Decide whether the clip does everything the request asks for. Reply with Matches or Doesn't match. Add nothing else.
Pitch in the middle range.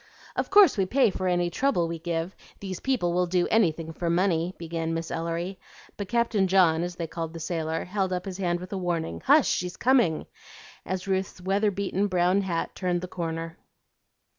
Matches